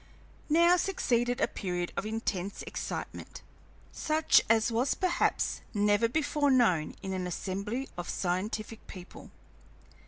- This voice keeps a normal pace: No, slow, 120 wpm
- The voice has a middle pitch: No, high, 220 Hz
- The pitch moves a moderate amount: No, wide, 6.1 semitones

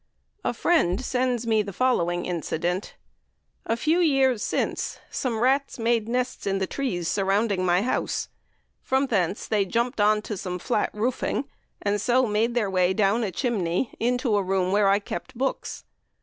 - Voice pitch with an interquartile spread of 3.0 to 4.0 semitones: No, average, 4.5 semitones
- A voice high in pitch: Yes, high, 215 Hz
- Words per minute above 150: Yes, average, 165 wpm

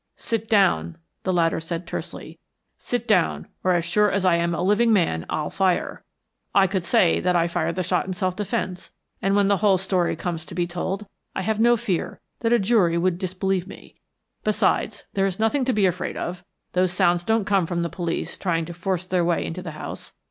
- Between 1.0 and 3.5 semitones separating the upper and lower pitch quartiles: Yes, narrow, 2.6 semitones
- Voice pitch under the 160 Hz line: No, medium, 185 Hz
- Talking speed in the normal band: No, fast, 215 wpm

